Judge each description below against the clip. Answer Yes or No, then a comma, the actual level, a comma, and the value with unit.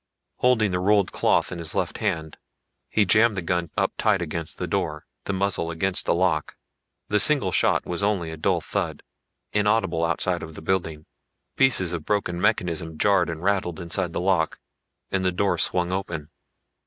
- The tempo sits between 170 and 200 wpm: Yes, average, 180 wpm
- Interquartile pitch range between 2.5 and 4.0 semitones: Yes, average, 3.2 semitones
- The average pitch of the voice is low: Yes, very low, 90 Hz